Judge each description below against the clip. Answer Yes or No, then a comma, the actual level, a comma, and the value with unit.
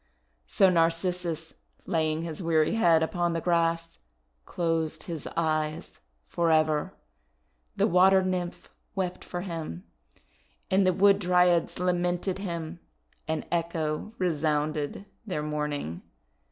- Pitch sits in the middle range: Yes, medium, 170 Hz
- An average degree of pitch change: No, narrow, 2.3 semitones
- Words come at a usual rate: No, slow, 110 wpm